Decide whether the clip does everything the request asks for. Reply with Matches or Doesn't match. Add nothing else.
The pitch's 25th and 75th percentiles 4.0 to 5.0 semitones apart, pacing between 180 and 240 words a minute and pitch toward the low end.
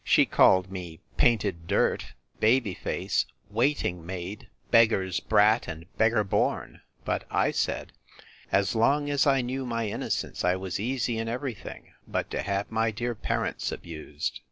Doesn't match